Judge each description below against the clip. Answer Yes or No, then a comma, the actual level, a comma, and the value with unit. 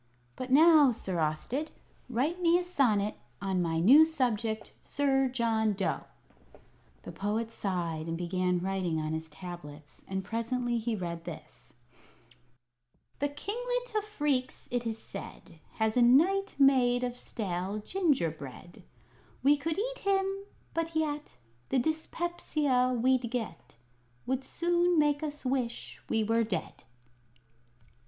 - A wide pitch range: Yes, wide, 7.6 semitones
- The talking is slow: Yes, slow, 130 wpm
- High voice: Yes, high, 245 Hz